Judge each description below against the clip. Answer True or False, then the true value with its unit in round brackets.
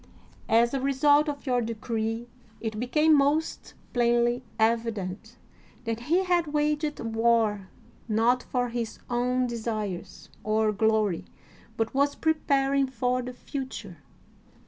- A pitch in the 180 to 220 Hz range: False (240 Hz)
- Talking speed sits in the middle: False (120 wpm)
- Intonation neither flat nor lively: True (3.8 semitones)